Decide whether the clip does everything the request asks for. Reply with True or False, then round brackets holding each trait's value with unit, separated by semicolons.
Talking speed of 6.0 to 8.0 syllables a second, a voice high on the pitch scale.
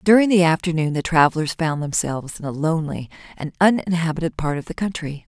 False (6.2 syllables/s; 165 Hz)